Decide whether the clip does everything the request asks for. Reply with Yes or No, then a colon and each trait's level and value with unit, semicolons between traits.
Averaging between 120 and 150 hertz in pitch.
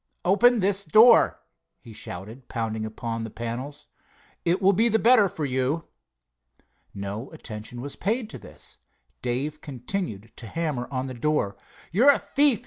Yes: medium, 140 Hz